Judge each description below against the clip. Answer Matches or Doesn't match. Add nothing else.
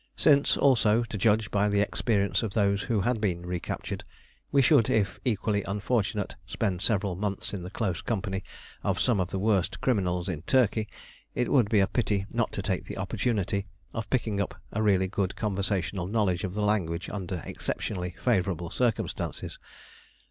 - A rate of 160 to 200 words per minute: Matches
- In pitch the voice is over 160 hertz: Doesn't match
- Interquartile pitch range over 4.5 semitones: Doesn't match